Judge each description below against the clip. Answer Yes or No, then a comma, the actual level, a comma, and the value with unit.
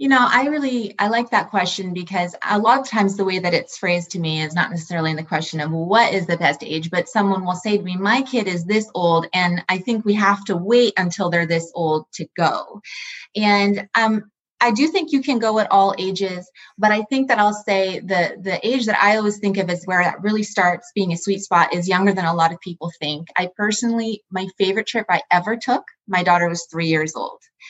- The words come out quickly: Yes, fast, 245 wpm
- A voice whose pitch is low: No, high, 195 Hz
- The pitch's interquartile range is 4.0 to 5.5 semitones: No, average, 3.5 semitones